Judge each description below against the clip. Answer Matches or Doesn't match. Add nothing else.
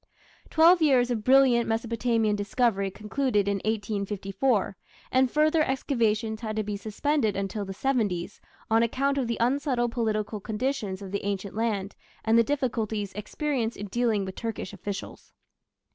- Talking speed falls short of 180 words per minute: Matches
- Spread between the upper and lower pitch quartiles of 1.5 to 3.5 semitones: Doesn't match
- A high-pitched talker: Matches